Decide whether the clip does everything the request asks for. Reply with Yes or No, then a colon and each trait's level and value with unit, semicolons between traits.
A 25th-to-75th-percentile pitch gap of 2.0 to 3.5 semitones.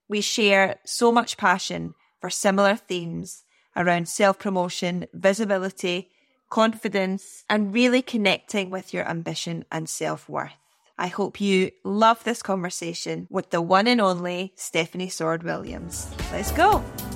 Yes: average, 2.8 semitones